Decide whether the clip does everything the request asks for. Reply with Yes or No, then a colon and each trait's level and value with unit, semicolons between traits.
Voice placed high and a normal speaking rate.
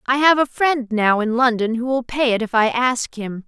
No: high, 245 Hz; fast, 260 wpm